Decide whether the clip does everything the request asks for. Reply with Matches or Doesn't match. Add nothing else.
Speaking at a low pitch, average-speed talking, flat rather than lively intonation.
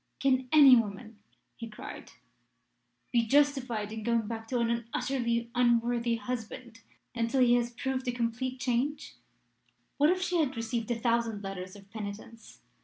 Doesn't match